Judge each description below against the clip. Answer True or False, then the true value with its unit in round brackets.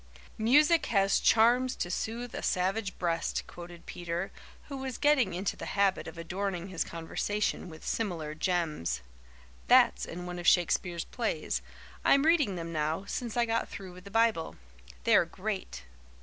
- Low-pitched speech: False (190 Hz)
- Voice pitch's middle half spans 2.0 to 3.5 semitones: False (4.9 semitones)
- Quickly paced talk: False (155 wpm)